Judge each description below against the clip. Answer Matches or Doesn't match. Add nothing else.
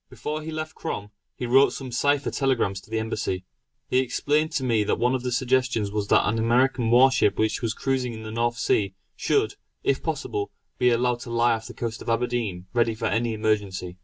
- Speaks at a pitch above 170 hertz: Doesn't match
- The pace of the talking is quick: Matches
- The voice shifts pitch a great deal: Doesn't match